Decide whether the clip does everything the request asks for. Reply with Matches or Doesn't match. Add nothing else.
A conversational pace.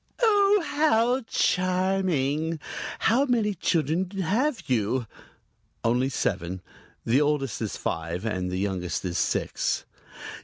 Doesn't match